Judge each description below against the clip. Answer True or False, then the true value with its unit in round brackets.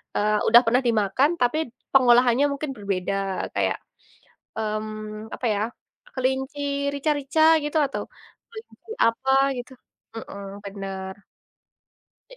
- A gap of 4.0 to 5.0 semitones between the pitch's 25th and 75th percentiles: True (4.3 semitones)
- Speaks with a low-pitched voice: False (240 Hz)